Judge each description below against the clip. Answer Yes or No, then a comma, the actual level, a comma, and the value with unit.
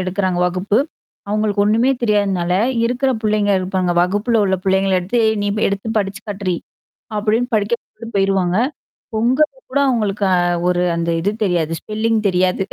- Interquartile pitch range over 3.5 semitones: No, average, 2.8 semitones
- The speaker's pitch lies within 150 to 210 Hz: Yes, high, 200 Hz